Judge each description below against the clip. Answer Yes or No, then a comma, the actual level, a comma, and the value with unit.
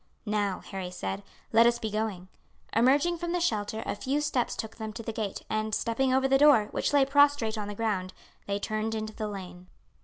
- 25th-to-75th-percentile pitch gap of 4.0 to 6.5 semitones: Yes, average, 4.3 semitones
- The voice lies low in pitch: No, high, 220 Hz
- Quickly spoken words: Yes, fast, 210 wpm